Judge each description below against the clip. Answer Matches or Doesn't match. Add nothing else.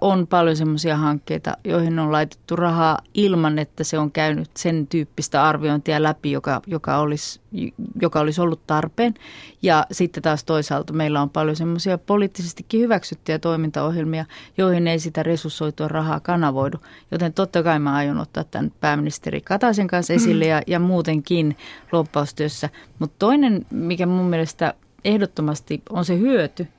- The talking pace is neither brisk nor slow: Matches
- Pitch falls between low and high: Matches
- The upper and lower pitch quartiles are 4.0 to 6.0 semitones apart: Doesn't match